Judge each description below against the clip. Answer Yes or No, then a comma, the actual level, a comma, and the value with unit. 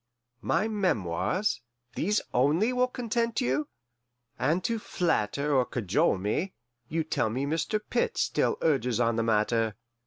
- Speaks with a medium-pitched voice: Yes, medium, 150 Hz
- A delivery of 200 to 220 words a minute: No, slow, 135 wpm